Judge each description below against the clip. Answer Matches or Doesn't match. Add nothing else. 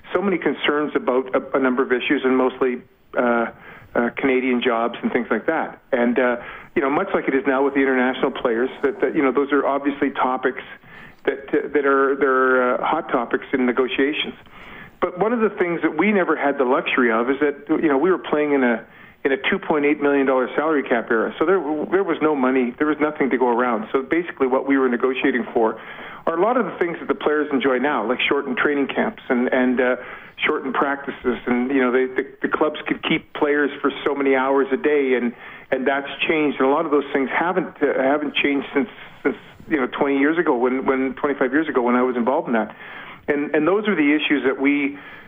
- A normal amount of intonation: Doesn't match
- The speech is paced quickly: Matches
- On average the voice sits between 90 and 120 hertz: Doesn't match